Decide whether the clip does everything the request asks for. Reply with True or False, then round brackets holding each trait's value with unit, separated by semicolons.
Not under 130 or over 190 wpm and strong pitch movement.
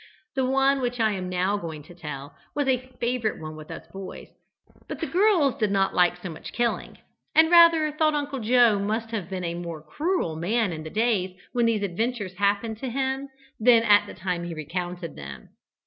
False (200 wpm; 6.3 semitones)